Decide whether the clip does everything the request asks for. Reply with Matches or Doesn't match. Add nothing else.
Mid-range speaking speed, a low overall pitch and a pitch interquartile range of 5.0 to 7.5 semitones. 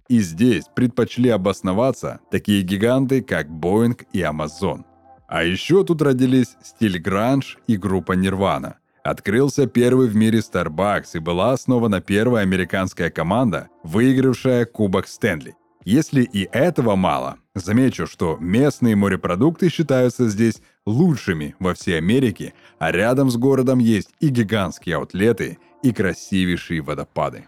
Matches